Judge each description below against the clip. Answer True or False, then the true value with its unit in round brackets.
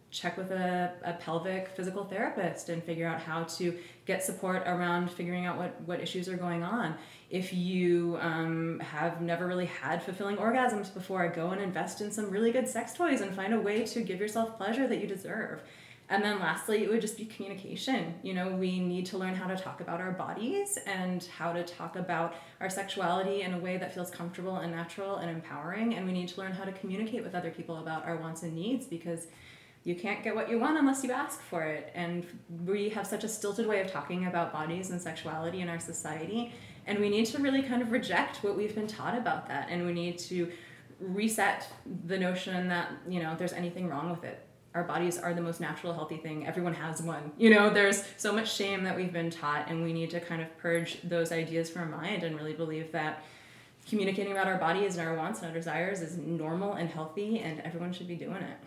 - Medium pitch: True (180 Hz)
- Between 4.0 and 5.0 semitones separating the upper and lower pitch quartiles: False (3.0 semitones)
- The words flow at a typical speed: False (225 wpm)